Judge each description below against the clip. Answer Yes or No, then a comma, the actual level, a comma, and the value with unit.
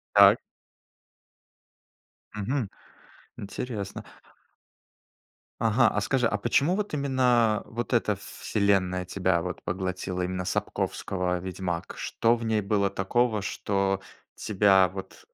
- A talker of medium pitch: No, low, 100 Hz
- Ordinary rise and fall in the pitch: Yes, average, 3.9 semitones